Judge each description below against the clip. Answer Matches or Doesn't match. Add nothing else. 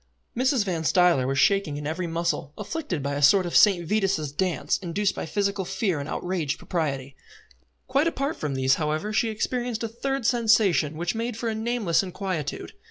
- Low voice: Doesn't match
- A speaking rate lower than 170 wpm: Doesn't match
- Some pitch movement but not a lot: Doesn't match